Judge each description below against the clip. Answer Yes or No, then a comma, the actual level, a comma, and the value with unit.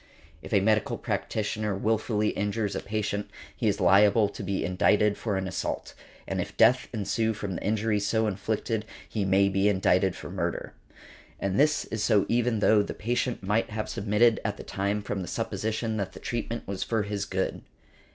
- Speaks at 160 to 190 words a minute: Yes, average, 185 wpm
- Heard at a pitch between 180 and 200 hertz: No, low, 105 Hz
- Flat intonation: Yes, narrow, 1.9 semitones